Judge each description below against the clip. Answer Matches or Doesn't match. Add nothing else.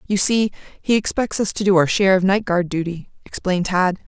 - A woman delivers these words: Matches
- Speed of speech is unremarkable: Doesn't match